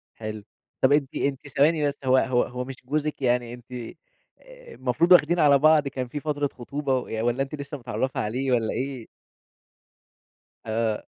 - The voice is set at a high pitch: No, low, 130 Hz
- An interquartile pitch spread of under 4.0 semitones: Yes, average, 2.9 semitones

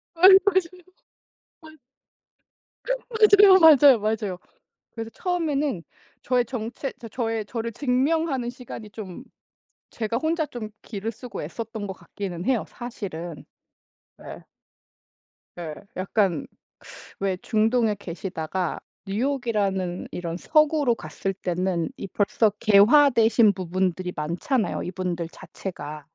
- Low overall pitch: No, high, 220 Hz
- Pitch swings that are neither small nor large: No, wide, 5.7 semitones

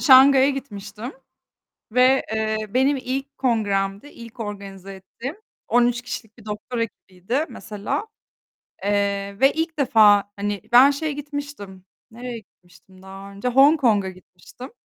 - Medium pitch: No, high, 225 Hz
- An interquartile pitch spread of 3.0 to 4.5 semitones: No, average, 5.0 semitones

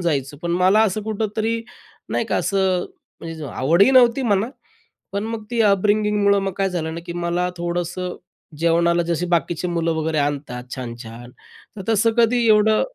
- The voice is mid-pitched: Yes, medium, 180 Hz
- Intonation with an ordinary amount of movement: Yes, average, 4.3 semitones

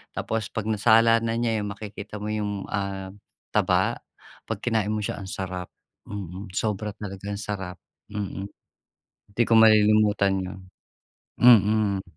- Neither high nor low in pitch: No, low, 105 Hz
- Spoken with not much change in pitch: Yes, narrow, 1.9 semitones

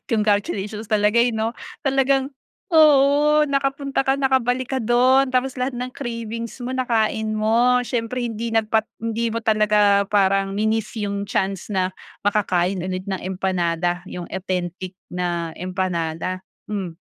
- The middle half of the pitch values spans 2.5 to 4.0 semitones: No, average, 4.7 semitones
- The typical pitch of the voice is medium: No, high, 215 Hz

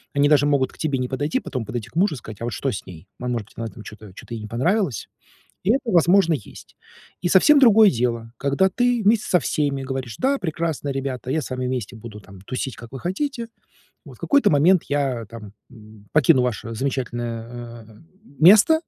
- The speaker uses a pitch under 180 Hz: Yes, low, 135 Hz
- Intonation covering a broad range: Yes, wide, 6.7 semitones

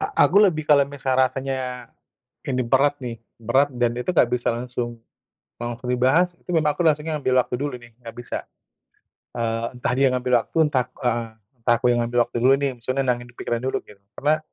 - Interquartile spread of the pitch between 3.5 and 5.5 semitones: No, average, 2.7 semitones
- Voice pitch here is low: Yes, low, 125 Hz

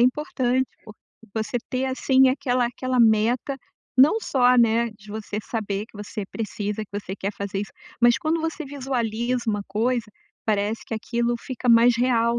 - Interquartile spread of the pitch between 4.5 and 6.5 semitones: No, average, 3.0 semitones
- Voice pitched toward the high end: Yes, high, 235 Hz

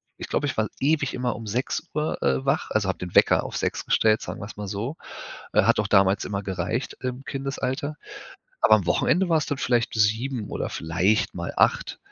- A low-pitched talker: Yes, low, 115 Hz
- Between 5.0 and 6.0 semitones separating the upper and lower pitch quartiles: Yes, average, 5.3 semitones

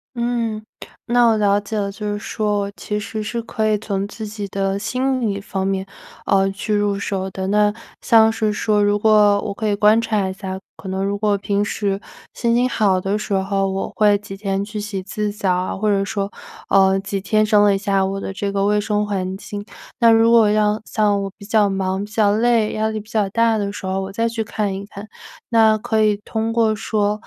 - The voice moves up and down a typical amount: No, narrow, 1.7 semitones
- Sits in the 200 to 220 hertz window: Yes, high, 205 Hz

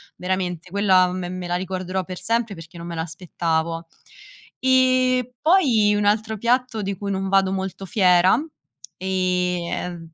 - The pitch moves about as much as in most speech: Yes, average, 3.1 semitones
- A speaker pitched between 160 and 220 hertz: Yes, high, 190 Hz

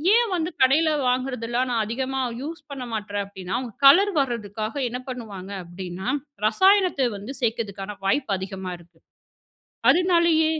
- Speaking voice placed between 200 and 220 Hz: No, high, 240 Hz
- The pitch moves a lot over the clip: Yes, wide, 6.0 semitones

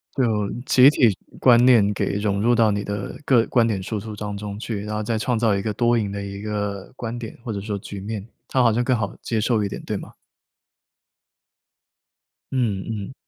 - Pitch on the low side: Yes, low, 105 Hz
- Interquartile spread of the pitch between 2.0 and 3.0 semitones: Yes, narrow, 2.6 semitones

